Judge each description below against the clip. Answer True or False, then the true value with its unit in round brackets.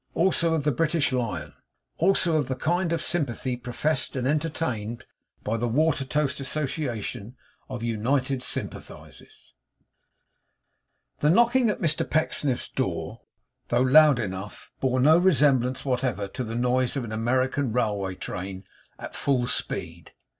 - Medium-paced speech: False (130 wpm)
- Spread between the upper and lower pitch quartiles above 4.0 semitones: True (4.4 semitones)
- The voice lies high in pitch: False (130 Hz)